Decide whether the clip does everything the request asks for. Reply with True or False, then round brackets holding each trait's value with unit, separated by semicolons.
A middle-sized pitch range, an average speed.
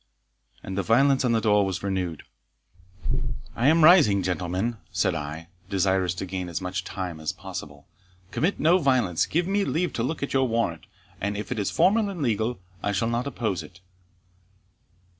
False (6.6 semitones; 180 wpm)